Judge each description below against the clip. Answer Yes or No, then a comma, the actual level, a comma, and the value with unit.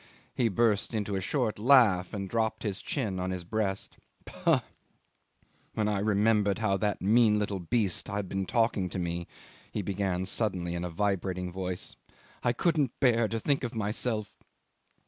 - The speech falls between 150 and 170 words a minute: Yes, average, 165 wpm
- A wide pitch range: No, average, 3.2 semitones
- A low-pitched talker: Yes, low, 105 Hz